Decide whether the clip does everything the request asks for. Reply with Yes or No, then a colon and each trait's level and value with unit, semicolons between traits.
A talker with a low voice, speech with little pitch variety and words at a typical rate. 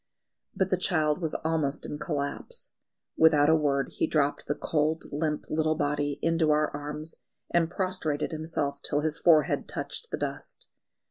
No: medium, 155 Hz; narrow, 1.8 semitones; average, 155 wpm